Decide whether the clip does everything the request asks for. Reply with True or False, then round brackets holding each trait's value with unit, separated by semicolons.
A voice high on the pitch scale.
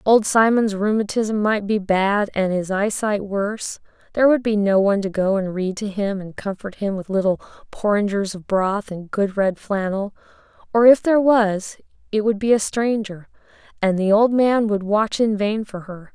True (205 Hz)